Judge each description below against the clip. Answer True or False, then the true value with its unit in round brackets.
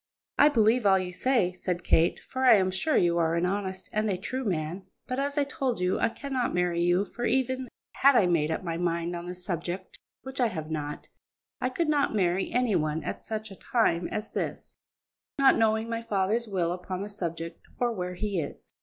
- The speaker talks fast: True (215 wpm)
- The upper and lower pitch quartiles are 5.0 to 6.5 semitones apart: True (5.3 semitones)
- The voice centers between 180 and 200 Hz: True (190 Hz)